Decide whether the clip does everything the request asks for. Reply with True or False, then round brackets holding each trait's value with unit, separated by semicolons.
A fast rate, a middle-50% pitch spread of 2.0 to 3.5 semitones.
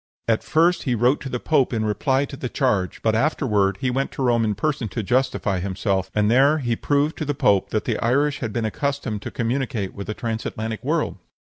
False (220 wpm; 4.3 semitones)